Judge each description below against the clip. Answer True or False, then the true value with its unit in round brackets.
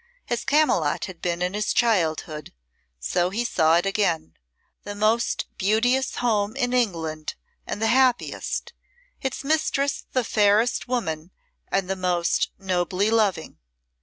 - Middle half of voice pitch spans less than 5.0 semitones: False (5.4 semitones)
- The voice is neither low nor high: False (205 Hz)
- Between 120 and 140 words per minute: True (135 wpm)